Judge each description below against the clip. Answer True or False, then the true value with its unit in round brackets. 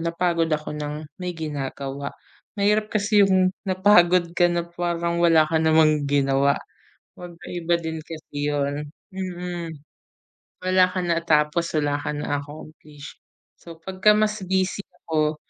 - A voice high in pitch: False (165 Hz)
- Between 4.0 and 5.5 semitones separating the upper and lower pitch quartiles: False (3.1 semitones)